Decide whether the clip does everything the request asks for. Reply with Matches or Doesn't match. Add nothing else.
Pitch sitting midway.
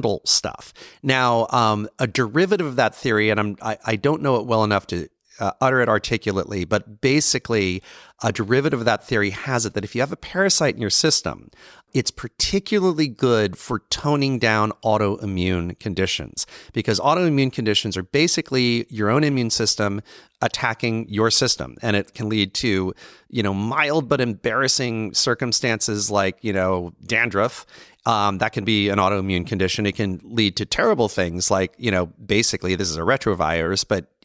Doesn't match